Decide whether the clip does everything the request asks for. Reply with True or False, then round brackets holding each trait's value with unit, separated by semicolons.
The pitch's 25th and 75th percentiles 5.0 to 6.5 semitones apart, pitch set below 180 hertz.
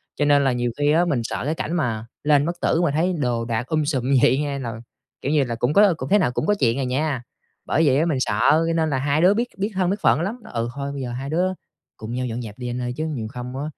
False (4.6 semitones; 140 Hz)